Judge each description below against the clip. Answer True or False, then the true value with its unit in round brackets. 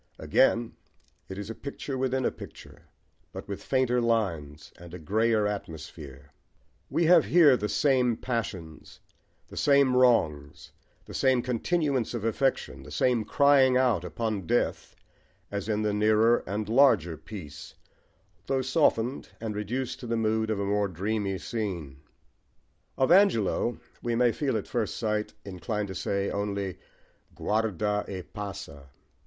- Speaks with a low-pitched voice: True (110 Hz)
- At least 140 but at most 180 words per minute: True (145 wpm)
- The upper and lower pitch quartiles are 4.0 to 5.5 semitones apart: True (4.3 semitones)